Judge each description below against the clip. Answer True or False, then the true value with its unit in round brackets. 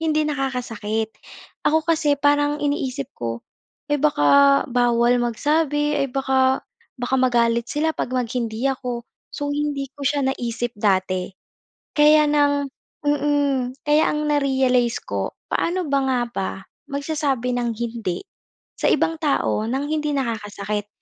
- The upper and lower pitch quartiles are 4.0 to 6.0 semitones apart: False (3.6 semitones)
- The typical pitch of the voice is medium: False (265 Hz)